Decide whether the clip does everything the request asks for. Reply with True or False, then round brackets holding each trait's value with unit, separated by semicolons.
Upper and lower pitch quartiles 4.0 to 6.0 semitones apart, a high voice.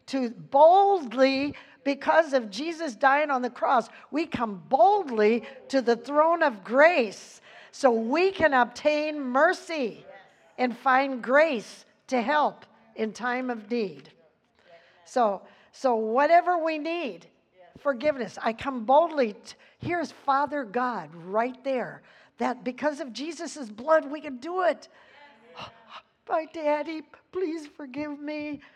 True (4.4 semitones; 275 Hz)